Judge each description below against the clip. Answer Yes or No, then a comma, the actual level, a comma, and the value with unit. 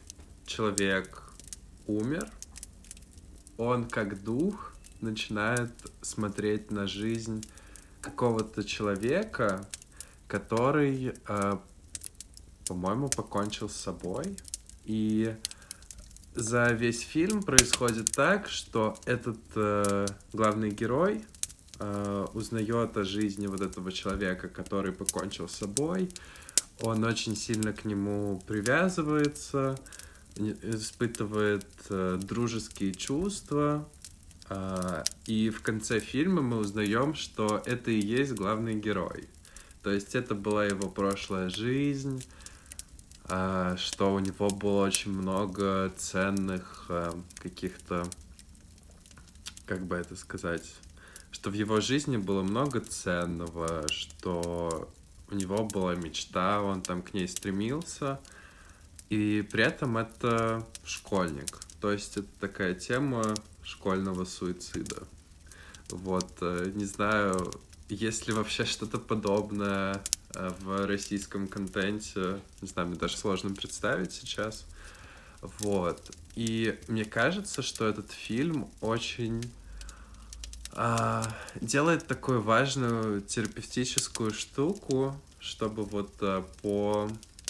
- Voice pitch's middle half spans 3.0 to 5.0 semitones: Yes, average, 3.8 semitones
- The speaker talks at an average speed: No, slow, 100 wpm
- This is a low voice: Yes, low, 100 Hz